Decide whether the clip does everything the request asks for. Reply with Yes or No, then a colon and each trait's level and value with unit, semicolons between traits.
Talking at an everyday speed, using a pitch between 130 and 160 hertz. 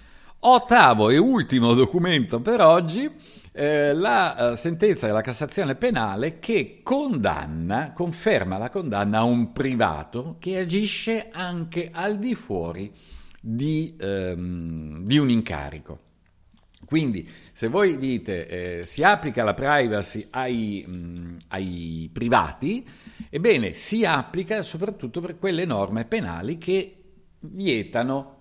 No: slow, 110 wpm; low, 135 Hz